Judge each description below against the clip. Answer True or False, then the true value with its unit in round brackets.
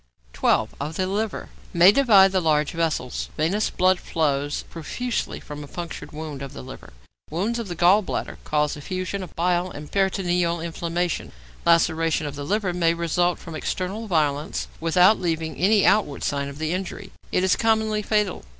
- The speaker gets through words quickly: False (170 wpm)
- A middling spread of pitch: True (3.5 semitones)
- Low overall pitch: False (175 Hz)